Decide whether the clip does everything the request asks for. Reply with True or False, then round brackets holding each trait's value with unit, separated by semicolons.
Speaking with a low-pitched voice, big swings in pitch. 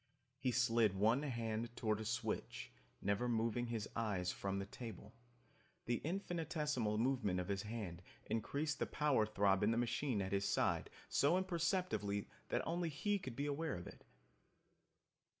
True (115 Hz; 5.8 semitones)